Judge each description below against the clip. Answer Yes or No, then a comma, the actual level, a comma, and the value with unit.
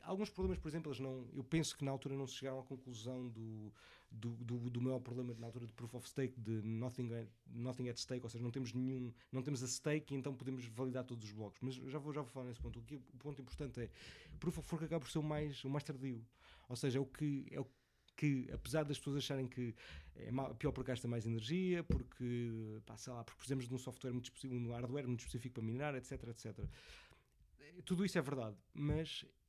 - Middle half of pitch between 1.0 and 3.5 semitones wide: Yes, average, 2.9 semitones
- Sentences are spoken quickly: Yes, fast, 240 wpm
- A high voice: No, low, 130 Hz